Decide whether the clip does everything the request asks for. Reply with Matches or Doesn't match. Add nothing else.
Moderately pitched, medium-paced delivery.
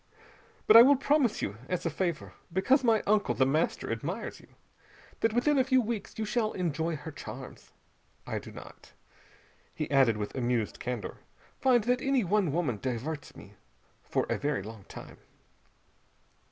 Matches